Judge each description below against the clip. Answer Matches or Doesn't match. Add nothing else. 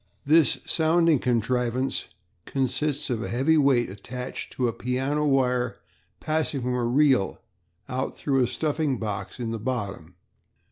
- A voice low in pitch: Matches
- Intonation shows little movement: Doesn't match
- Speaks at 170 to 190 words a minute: Doesn't match